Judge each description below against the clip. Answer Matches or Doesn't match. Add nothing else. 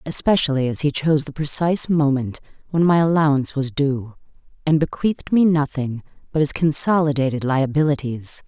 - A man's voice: Doesn't match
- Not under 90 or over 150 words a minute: Matches